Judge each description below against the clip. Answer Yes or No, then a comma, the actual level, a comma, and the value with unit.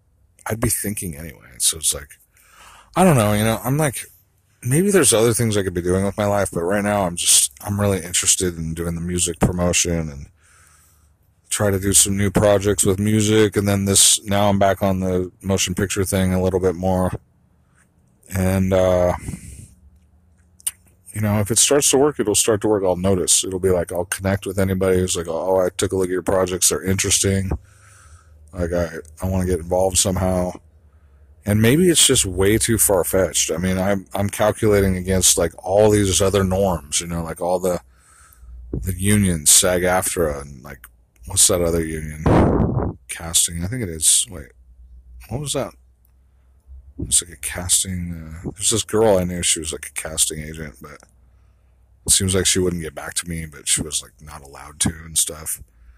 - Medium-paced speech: Yes, average, 195 wpm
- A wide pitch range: No, average, 3.1 semitones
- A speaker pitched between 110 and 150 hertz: No, very low, 90 Hz